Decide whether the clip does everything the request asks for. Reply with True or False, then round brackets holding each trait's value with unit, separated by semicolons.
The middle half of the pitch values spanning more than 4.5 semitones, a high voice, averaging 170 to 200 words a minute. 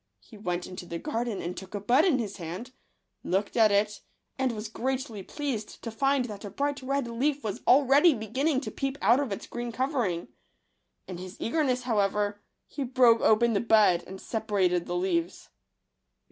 True (4.9 semitones; 225 Hz; 180 wpm)